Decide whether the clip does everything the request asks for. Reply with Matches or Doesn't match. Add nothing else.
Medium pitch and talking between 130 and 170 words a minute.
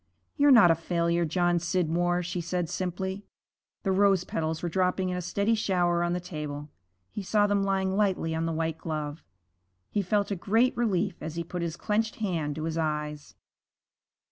Doesn't match